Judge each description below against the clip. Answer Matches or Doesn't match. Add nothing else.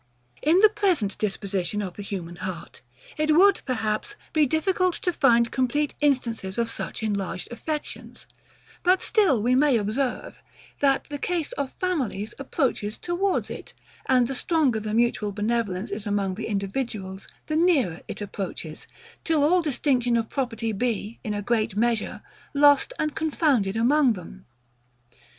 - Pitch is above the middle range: Matches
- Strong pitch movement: Matches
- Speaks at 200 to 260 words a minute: Doesn't match